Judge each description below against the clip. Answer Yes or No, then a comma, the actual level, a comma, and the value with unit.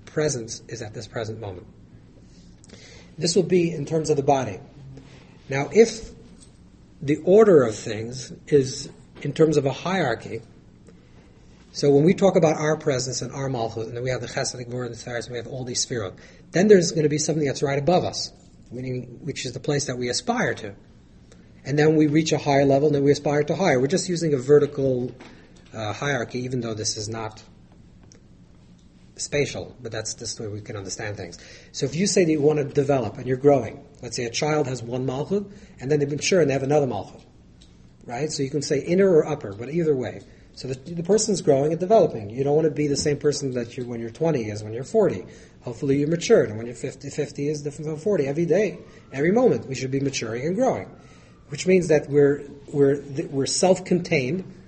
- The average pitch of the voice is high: No, medium, 140 Hz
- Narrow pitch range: No, average, 4.5 semitones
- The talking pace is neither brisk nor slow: No, fast, 215 wpm